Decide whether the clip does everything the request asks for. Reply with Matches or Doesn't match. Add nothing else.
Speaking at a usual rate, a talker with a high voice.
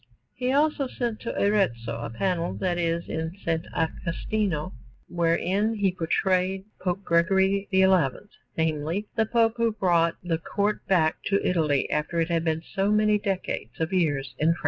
Doesn't match